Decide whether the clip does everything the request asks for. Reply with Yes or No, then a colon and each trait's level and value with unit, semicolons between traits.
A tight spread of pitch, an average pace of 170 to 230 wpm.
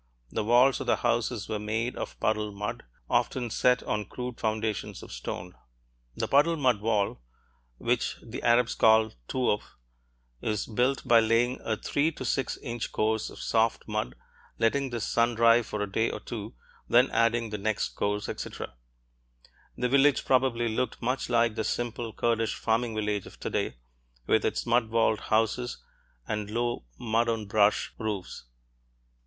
No: narrow, 2.1 semitones; average, 160 wpm